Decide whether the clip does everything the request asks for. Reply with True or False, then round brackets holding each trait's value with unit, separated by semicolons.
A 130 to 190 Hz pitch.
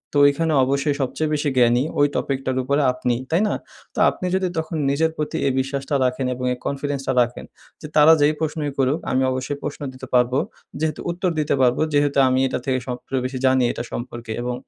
True (135 Hz)